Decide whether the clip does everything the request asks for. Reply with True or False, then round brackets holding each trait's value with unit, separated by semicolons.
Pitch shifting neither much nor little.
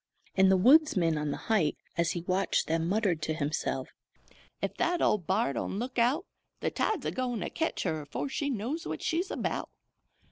False (7.9 semitones)